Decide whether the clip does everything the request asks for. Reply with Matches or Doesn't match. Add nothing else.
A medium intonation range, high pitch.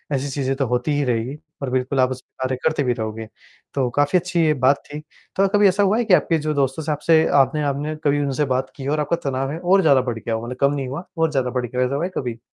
Doesn't match